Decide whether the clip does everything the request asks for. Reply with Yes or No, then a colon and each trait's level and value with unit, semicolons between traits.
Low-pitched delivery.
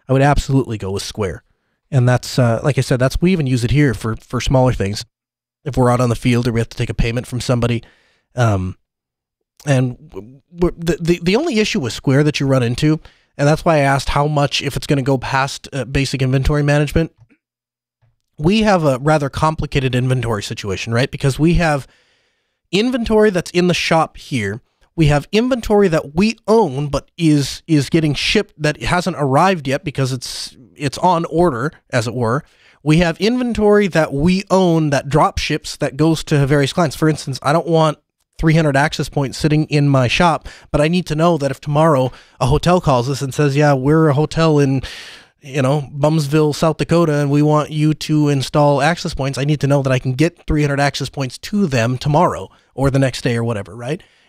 No: medium, 145 Hz